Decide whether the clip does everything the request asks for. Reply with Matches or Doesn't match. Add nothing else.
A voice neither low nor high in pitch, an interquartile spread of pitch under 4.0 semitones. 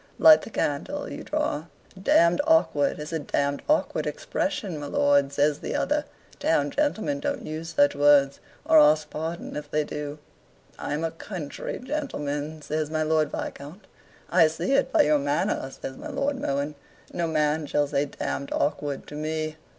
Matches